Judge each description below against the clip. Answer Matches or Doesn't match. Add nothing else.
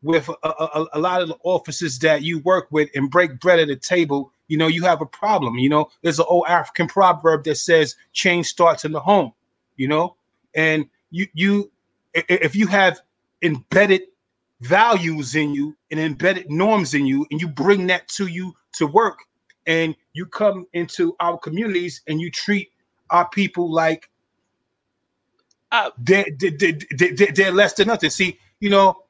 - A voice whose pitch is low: Doesn't match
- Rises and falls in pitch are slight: Doesn't match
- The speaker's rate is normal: Matches